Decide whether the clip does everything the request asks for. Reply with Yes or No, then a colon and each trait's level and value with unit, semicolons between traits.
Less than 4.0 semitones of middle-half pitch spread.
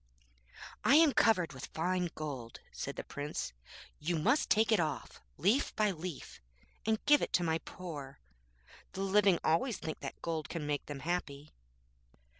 No: average, 5.3 semitones